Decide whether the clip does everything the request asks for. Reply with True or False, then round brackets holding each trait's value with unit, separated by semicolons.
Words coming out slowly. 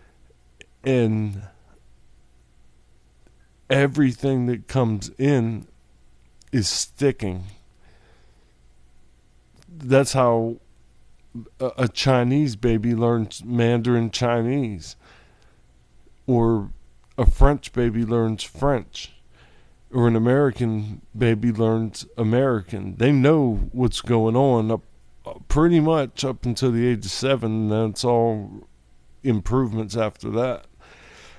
True (90 wpm)